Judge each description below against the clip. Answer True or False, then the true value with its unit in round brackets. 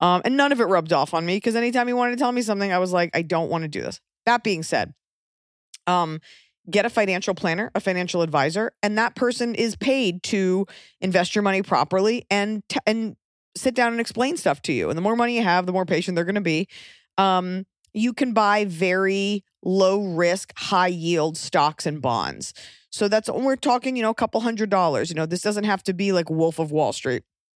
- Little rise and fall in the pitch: False (4.2 semitones)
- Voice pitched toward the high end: True (195 Hz)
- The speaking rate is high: True (230 wpm)